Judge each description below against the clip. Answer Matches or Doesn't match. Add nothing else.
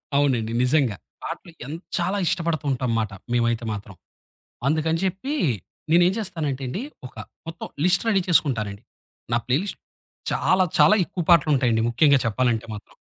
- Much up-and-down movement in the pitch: Matches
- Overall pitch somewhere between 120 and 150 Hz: Matches